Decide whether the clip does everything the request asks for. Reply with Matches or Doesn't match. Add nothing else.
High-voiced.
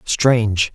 Doesn't match